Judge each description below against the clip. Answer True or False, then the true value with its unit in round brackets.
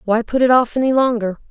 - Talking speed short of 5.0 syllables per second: False (6.1 syllables/s)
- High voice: True (240 Hz)